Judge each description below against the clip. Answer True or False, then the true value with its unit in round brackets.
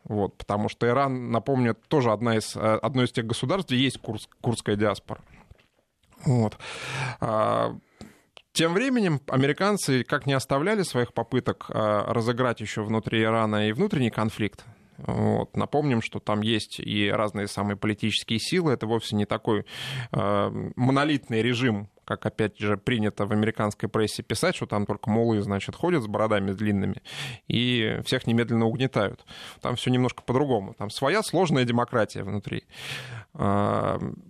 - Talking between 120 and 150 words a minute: True (140 wpm)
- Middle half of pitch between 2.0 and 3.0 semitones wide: False (3.6 semitones)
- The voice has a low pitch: True (115 Hz)